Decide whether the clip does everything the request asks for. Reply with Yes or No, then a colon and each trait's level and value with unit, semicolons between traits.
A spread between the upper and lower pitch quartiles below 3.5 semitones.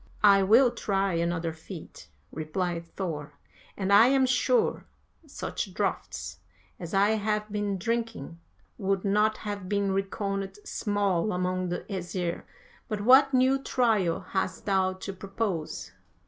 Yes: average, 2.8 semitones